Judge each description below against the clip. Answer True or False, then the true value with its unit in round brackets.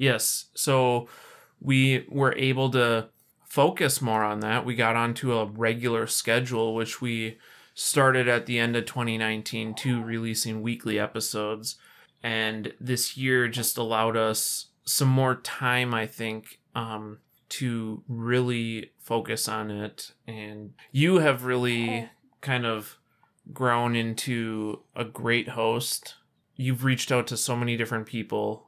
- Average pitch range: False (2.1 semitones)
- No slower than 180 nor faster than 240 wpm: False (135 wpm)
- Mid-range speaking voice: False (115 Hz)